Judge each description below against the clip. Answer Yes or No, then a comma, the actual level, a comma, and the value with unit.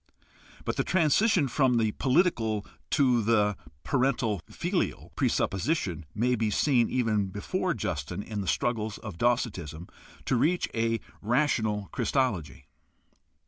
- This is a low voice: Yes, low, 115 Hz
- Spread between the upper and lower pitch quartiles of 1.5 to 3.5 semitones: No, average, 4.2 semitones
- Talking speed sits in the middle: No, slow, 120 wpm